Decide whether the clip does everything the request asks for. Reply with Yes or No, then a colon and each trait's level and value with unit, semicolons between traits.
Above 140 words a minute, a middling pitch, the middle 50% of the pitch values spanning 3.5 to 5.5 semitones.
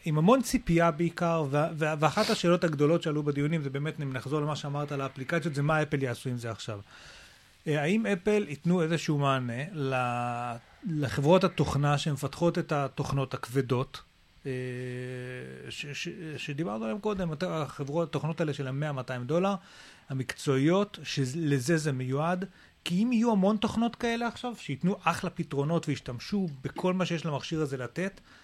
Yes: fast, 150 wpm; medium, 150 Hz; average, 4.1 semitones